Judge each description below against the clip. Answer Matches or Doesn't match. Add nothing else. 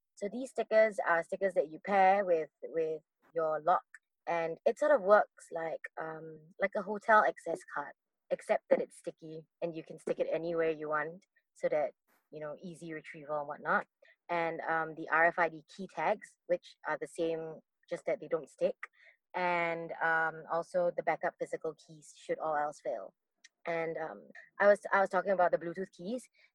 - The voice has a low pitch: Doesn't match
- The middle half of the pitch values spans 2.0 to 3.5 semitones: Doesn't match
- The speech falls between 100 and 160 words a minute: Doesn't match